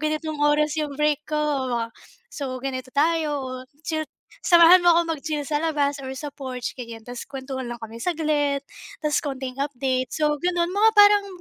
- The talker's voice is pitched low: No, very high, 295 Hz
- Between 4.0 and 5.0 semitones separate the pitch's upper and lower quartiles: No, average, 3.1 semitones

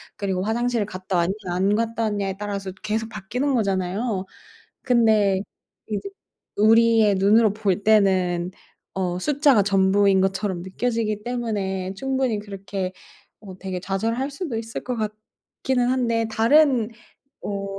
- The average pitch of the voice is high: Yes, high, 210 Hz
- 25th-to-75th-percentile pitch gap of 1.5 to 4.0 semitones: Yes, average, 3.1 semitones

